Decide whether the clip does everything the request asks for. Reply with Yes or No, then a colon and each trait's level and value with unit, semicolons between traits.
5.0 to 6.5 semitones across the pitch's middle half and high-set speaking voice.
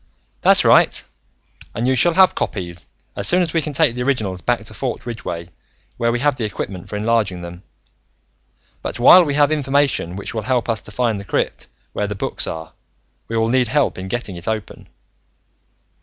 No: wide, 5.6 semitones; low, 115 Hz